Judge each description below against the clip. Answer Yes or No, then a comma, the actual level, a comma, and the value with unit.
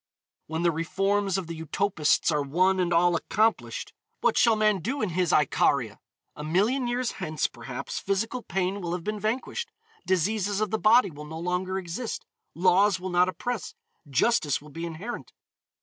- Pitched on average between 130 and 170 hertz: No, medium, 185 Hz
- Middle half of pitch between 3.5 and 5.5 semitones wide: Yes, average, 4.2 semitones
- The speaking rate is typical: Yes, average, 170 wpm